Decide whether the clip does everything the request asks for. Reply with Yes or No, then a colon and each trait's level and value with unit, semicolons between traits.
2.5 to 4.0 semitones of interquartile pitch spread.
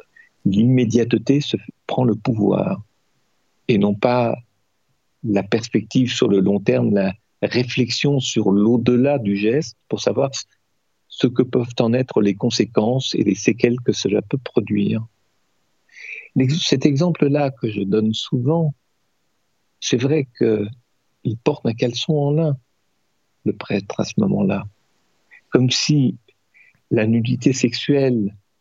Yes: average, 3.7 semitones